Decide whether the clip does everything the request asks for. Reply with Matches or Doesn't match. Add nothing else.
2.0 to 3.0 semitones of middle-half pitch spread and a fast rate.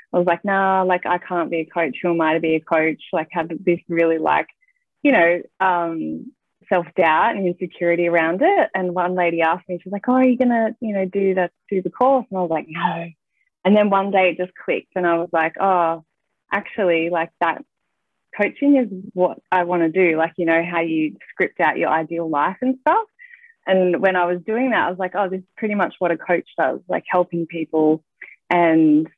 Matches